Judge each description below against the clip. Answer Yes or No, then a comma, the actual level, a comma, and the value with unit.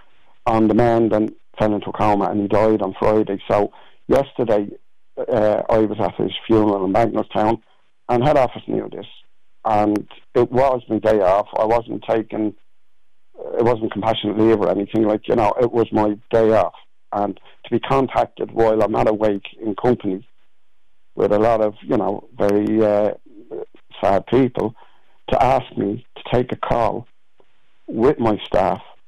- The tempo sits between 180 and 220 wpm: No, average, 165 wpm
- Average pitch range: No, narrow, 1.7 semitones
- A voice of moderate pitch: No, low, 110 Hz